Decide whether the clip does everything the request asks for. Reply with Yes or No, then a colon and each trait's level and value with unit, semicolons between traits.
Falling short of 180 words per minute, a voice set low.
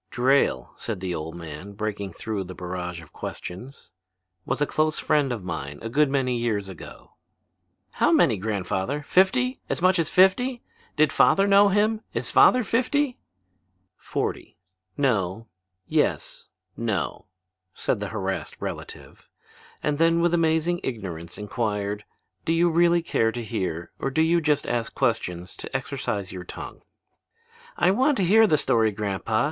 Yes: average, 150 wpm; low, 120 Hz